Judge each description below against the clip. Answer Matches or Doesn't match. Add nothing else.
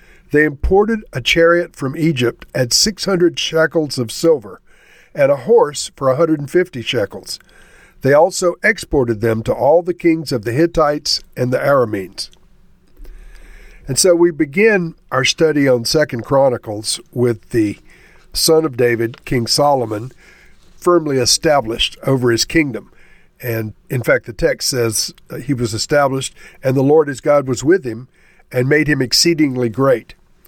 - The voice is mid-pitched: Matches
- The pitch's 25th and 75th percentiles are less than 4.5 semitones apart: Doesn't match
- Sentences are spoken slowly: Doesn't match